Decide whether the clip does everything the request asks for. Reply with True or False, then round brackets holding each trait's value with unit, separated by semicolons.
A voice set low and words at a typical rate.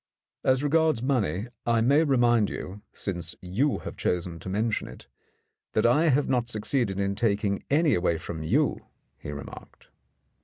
True (110 Hz; 155 wpm)